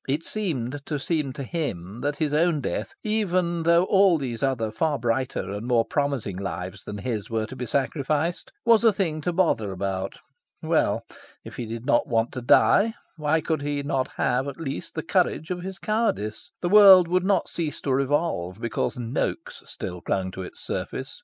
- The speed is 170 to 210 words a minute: Yes, average, 190 wpm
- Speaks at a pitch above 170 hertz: No, medium, 140 Hz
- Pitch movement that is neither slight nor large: No, wide, 6.8 semitones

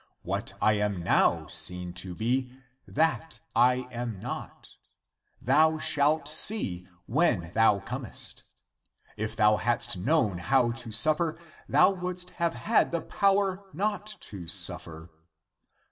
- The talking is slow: Yes, slow, 125 wpm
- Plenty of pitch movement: Yes, wide, 7.9 semitones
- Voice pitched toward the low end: Yes, low, 125 Hz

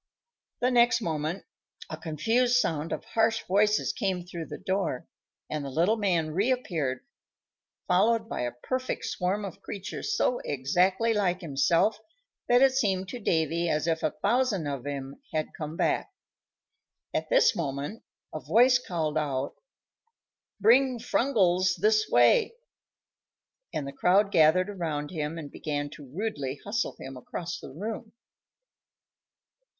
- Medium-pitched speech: Yes, medium, 180 Hz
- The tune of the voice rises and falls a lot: Yes, wide, 6.4 semitones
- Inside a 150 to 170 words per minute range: No, average, 140 wpm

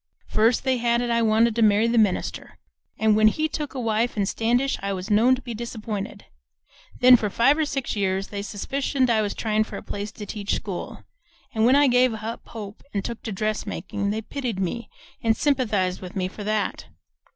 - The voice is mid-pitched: No, high, 220 Hz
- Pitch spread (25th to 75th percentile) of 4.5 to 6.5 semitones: No, average, 2.9 semitones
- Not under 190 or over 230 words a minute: Yes, fast, 205 wpm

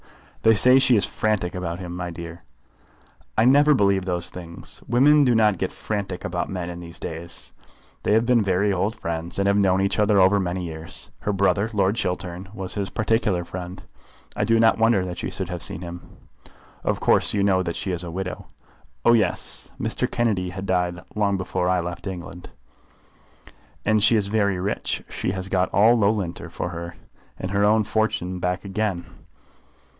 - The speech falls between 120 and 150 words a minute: No, average, 190 wpm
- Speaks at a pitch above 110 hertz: No, very low, 95 Hz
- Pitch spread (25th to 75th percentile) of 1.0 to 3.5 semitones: Yes, average, 3.2 semitones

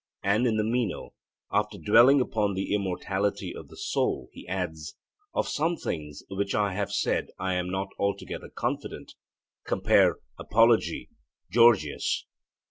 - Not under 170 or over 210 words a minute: No, slow, 135 wpm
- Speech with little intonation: No, average, 3.2 semitones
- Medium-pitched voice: No, low, 100 Hz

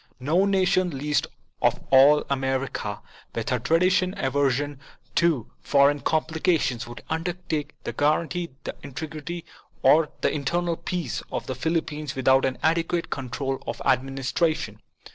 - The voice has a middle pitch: Yes, medium, 150 Hz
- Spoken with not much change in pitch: No, average, 3.9 semitones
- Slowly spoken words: Yes, slow, 130 wpm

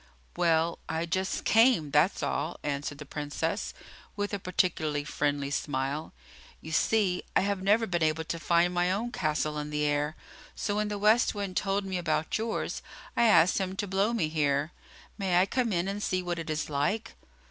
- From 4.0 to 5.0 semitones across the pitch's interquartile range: Yes, average, 4.7 semitones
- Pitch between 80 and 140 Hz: No, medium, 175 Hz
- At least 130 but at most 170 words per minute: No, average, 190 wpm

